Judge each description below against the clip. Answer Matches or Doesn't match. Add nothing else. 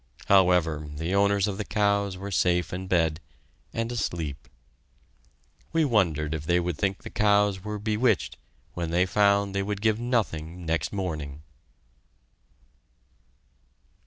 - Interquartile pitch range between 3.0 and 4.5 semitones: Matches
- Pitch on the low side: Matches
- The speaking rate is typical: Doesn't match